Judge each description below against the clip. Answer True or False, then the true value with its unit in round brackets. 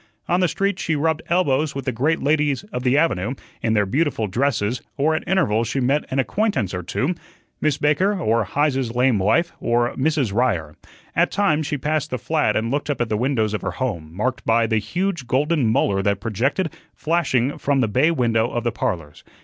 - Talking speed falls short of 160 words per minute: False (205 wpm)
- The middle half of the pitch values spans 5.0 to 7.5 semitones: True (5.3 semitones)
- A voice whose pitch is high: False (130 Hz)